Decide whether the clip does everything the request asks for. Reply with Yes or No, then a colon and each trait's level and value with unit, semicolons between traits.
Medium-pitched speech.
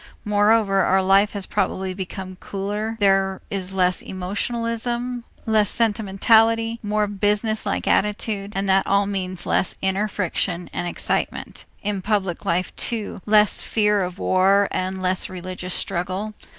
No: high, 200 Hz